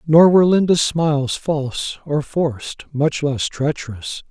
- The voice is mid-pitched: Yes, medium, 150 Hz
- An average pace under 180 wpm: Yes, average, 140 wpm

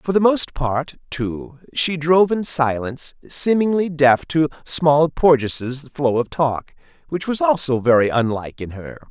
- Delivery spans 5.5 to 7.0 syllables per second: No, 4.2 syllables/s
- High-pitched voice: No, medium, 145 Hz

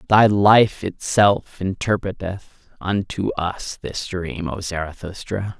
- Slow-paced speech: Yes, slow, 105 wpm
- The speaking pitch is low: Yes, very low, 95 Hz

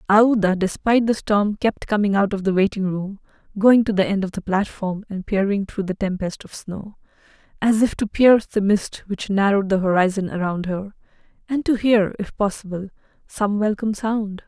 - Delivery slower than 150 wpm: No, average, 185 wpm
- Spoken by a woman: Yes, female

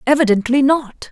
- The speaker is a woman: Yes, female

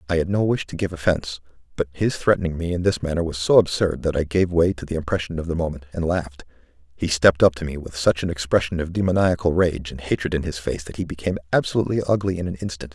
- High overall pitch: No, very low, 85 Hz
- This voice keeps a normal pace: No, fast, 245 wpm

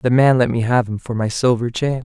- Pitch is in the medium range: No, low, 120 Hz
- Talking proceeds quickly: Yes, fast, 285 wpm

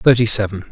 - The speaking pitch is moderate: No, low, 110 Hz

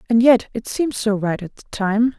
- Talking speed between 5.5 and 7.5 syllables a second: No, 5.3 syllables/s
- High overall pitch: Yes, high, 225 Hz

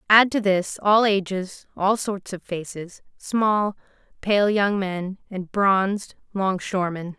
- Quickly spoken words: No, slow, 135 wpm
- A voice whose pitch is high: Yes, high, 195 Hz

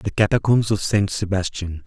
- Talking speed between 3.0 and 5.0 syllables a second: Yes, 4.9 syllables/s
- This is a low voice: Yes, low, 100 Hz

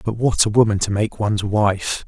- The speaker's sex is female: No, male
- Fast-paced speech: Yes, fast, 230 wpm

